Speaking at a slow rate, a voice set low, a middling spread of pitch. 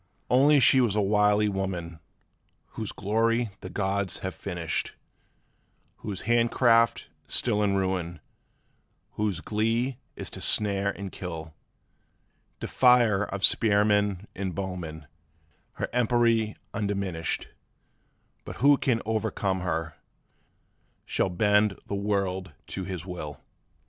Yes: slow, 110 wpm; low, 100 Hz; average, 3.1 semitones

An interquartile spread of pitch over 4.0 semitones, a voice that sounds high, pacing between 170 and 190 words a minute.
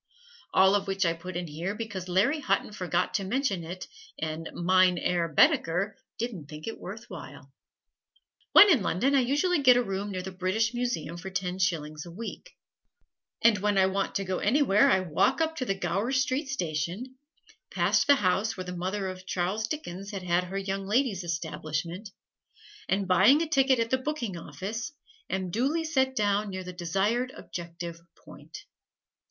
Yes: average, 4.7 semitones; high, 195 Hz; average, 175 wpm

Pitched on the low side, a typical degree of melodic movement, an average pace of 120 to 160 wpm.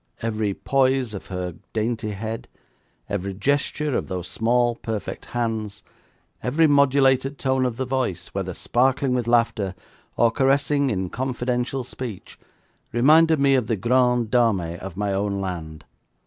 Yes: low, 120 Hz; average, 4.6 semitones; average, 140 wpm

